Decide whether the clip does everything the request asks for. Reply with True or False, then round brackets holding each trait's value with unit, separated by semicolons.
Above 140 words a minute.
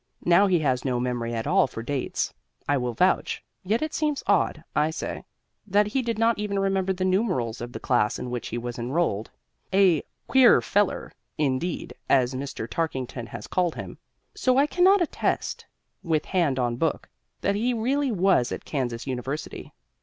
True (175 wpm)